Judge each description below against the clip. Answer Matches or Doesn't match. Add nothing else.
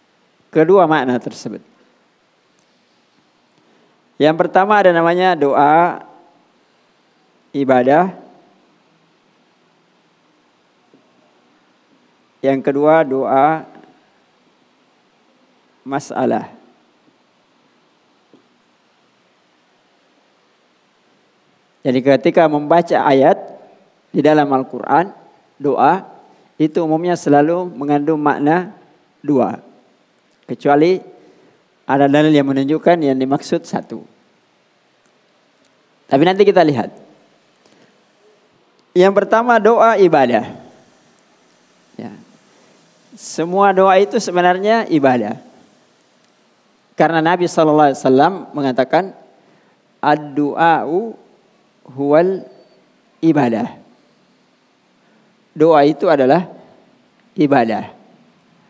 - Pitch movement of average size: Matches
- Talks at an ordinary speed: Doesn't match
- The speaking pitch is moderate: Matches